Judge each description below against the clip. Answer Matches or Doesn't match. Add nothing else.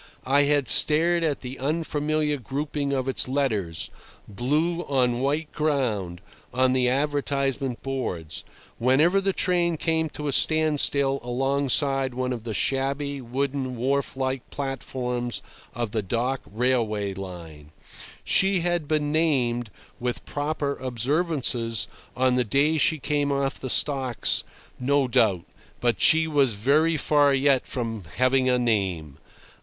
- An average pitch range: Matches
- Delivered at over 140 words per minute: Doesn't match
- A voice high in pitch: Doesn't match